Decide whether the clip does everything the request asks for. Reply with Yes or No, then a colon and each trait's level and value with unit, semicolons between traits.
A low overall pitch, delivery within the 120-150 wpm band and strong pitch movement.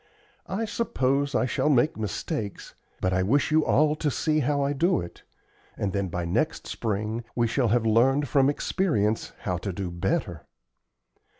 No: low, 125 Hz; average, 170 wpm; wide, 6.3 semitones